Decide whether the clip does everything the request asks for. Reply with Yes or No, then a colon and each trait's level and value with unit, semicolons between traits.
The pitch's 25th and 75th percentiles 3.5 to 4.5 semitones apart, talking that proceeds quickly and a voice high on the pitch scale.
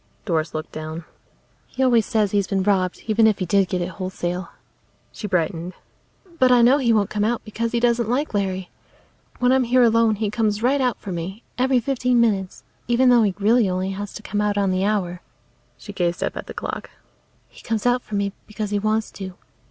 Yes: average, 3.9 semitones; fast, 215 wpm; high, 210 Hz